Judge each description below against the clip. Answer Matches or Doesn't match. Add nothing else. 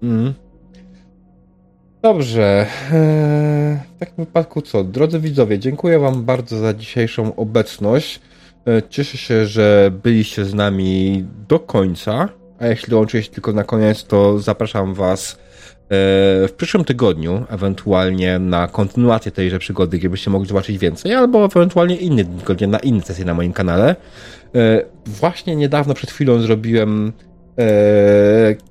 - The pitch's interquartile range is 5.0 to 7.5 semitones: Matches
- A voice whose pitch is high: Doesn't match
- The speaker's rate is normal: Matches